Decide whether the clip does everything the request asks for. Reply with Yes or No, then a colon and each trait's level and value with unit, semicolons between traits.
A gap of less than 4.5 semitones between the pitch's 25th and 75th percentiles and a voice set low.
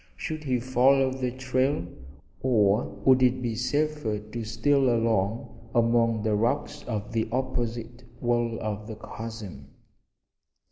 Yes: average, 2.7 semitones; low, 120 Hz